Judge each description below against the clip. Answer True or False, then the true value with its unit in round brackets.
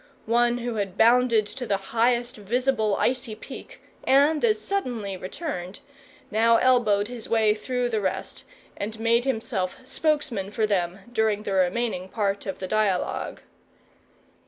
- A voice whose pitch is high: True (225 Hz)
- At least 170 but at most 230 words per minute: False (140 wpm)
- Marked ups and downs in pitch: False (3.4 semitones)